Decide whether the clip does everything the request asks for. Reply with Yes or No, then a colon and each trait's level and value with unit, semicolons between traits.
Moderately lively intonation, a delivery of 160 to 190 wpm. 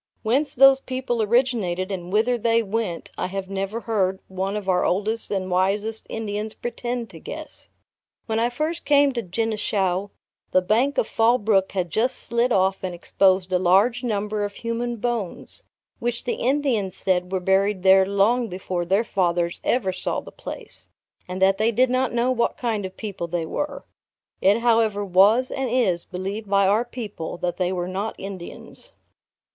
Yes: average, 4.0 semitones; average, 175 wpm